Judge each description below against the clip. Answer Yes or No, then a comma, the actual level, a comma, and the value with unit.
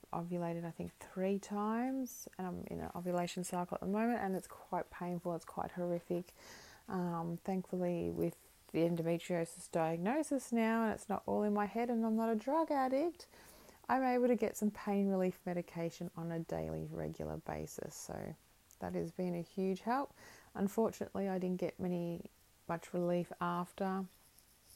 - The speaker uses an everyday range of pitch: Yes, average, 4.0 semitones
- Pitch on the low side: No, medium, 180 Hz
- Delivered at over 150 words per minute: Yes, average, 165 wpm